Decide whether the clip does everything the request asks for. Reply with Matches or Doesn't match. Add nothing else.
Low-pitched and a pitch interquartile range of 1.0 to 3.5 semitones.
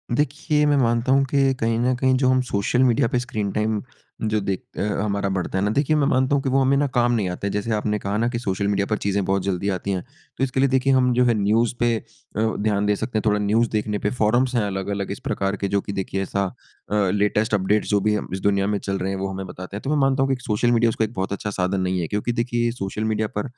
Doesn't match